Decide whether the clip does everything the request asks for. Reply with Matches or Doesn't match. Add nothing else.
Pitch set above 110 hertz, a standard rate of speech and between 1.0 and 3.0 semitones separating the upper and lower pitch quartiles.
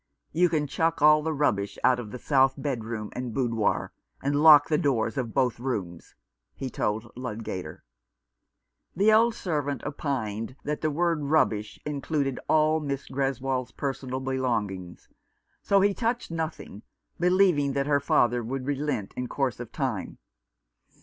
Doesn't match